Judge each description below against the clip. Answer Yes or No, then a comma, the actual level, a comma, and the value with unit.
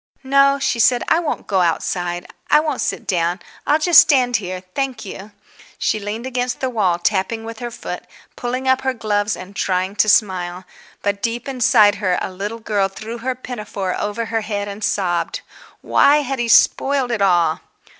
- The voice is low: No, high, 220 Hz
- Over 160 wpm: Yes, average, 185 wpm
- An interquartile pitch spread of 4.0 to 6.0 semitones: Yes, average, 4.7 semitones